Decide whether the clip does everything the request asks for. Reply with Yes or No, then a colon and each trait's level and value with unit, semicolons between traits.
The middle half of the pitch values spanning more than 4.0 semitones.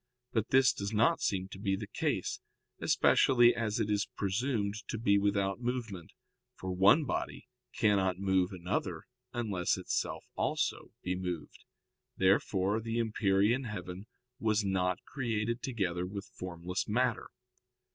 No: average, 3.3 semitones